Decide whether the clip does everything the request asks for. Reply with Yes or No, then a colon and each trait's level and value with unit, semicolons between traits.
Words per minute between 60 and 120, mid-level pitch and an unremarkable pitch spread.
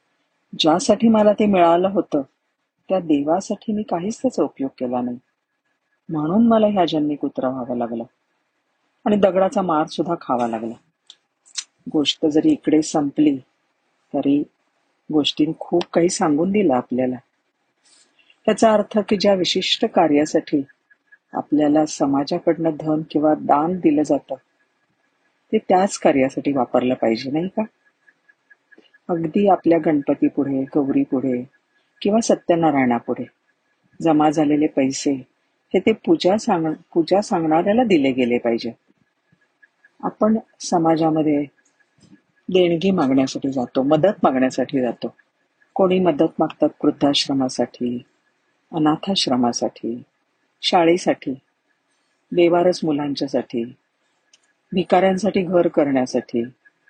No: average, 100 wpm; medium, 165 Hz; wide, 6.6 semitones